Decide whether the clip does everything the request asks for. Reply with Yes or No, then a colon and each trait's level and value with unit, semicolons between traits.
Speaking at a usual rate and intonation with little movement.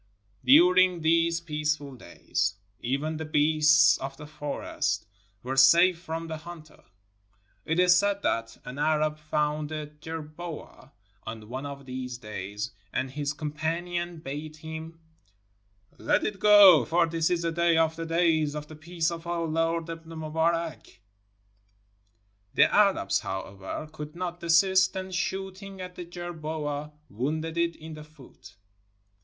Yes: average, 145 wpm; narrow, 2.3 semitones